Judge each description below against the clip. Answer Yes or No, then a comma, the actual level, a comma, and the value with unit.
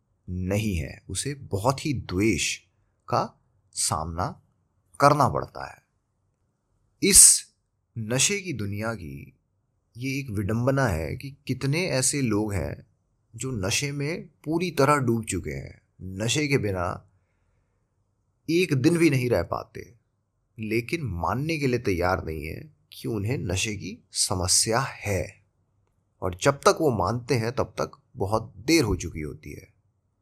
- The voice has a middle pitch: No, low, 110 Hz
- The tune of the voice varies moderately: No, wide, 5.7 semitones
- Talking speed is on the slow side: No, average, 135 wpm